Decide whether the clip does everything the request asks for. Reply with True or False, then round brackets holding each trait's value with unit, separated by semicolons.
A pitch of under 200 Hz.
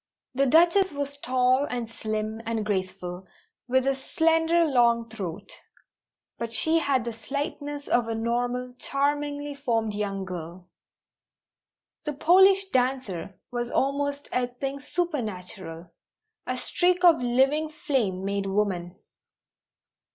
False (250 Hz)